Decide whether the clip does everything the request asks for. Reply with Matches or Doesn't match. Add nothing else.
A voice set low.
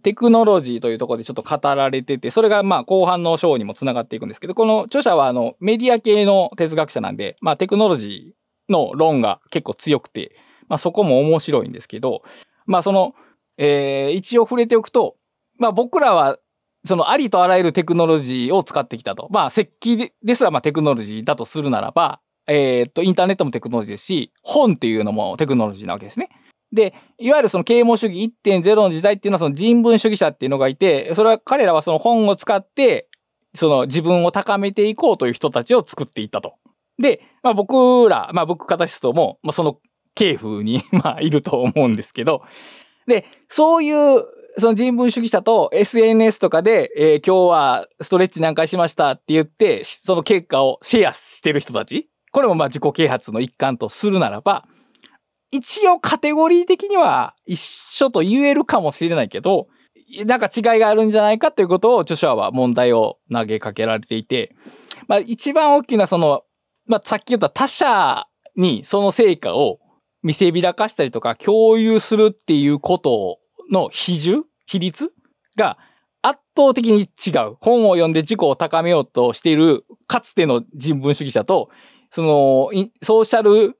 Doesn't match